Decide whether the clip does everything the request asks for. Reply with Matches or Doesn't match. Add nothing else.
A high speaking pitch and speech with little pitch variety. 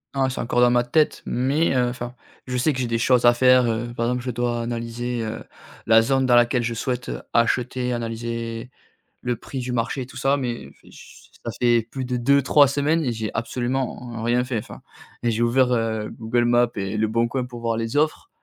Doesn't match